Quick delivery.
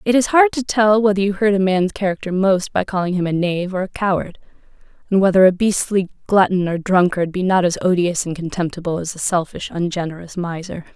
Yes: fast, 210 wpm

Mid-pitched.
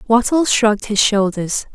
No: high, 220 Hz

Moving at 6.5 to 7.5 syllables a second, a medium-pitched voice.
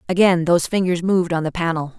Yes: 6.7 syllables/s; medium, 175 Hz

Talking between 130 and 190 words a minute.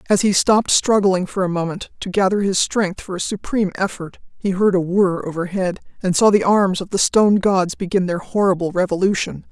No: average, 200 wpm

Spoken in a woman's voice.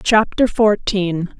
Yes: female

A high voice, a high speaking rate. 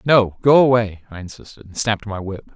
No: low, 110 Hz; fast, 210 wpm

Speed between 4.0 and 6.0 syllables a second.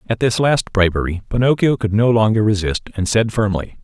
Yes: 5.5 syllables/s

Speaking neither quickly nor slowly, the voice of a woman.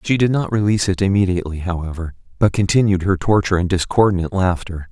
No: average, 170 wpm; male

